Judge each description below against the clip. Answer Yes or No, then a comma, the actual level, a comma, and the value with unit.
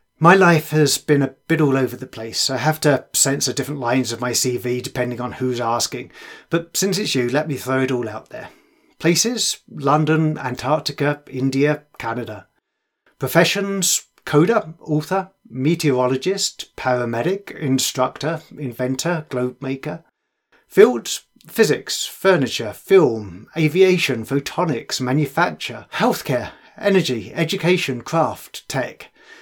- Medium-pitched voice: Yes, medium, 145 Hz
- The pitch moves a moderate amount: Yes, average, 4.7 semitones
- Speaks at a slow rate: Yes, slow, 120 wpm